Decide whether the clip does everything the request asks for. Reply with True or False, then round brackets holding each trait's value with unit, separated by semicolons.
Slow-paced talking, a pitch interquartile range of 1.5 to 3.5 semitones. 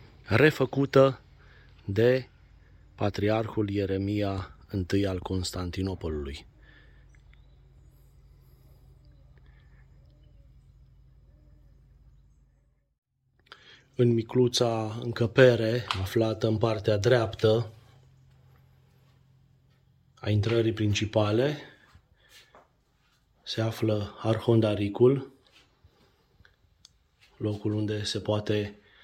False (50 wpm; 4.0 semitones)